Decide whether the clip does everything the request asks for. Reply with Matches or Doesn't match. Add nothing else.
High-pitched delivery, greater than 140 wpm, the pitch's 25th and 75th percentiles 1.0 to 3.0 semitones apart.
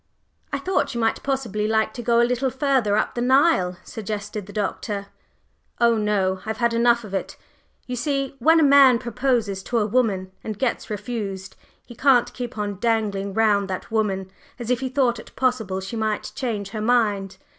Doesn't match